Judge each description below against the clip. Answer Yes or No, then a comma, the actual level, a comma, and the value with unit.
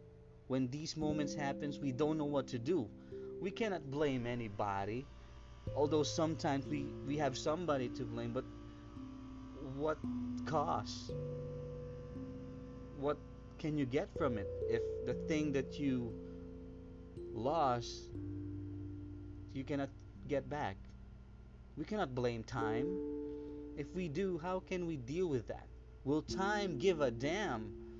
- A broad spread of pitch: No, average, 4.8 semitones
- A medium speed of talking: No, slow, 125 wpm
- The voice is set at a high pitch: No, low, 130 Hz